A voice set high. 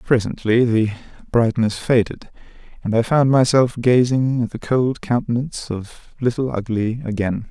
No: low, 120 Hz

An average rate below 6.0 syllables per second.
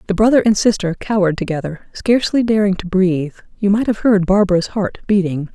No: 6.1 syllables/s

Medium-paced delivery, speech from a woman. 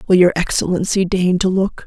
Yes: average, 195 wpm; female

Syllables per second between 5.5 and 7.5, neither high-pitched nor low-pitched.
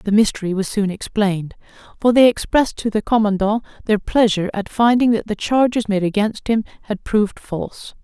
No: 5.6 syllables/s; high, 215 Hz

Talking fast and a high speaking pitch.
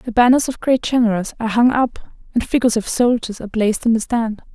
Yes: fast, 225 wpm; high, 230 Hz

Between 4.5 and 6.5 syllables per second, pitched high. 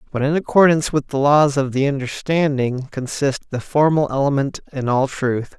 No: 5.0 syllables/s; medium, 140 Hz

